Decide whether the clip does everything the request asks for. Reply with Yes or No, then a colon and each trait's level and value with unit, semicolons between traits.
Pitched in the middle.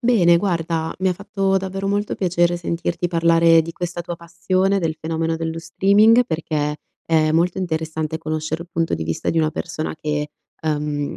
Yes: medium, 165 Hz